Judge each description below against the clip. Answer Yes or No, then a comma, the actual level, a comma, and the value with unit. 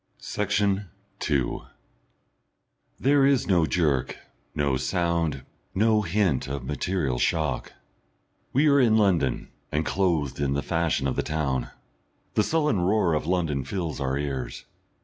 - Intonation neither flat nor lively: No, wide, 6.3 semitones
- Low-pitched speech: Yes, very low, 85 Hz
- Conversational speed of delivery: No, slow, 130 wpm